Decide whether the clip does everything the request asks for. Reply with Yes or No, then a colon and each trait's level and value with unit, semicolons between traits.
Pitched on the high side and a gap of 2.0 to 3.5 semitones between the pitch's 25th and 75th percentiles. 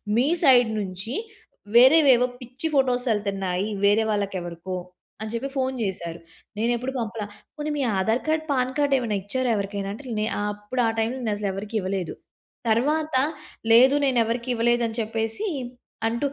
No: high, 230 Hz; average, 3.9 semitones